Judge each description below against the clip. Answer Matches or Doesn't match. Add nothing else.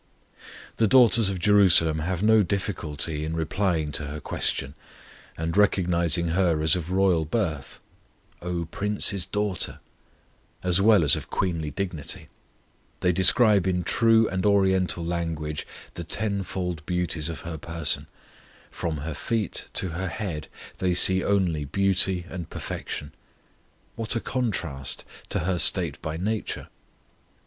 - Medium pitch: Doesn't match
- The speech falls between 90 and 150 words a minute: Matches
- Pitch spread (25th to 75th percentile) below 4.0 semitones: Matches